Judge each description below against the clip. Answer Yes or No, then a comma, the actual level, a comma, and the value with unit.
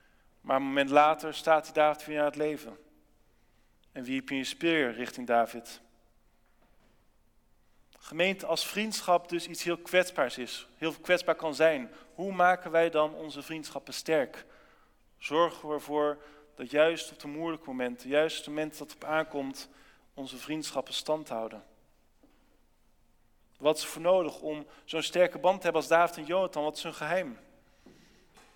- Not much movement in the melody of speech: No, average, 3.1 semitones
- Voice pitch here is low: No, medium, 155 Hz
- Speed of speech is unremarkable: Yes, average, 165 wpm